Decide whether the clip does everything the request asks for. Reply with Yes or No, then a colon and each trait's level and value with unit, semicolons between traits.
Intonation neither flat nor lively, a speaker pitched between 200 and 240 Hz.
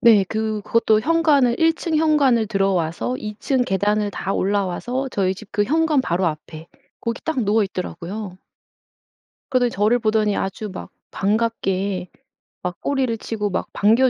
Yes: average, 4.3 semitones; high, 215 Hz